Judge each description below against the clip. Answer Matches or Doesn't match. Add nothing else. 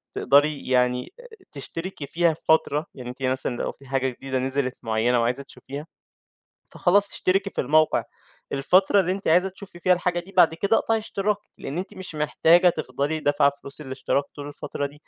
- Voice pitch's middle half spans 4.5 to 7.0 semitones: Matches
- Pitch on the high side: Doesn't match